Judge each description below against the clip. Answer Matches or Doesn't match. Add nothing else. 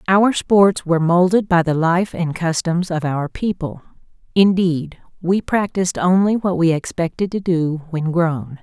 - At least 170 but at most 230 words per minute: Doesn't match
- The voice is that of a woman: Matches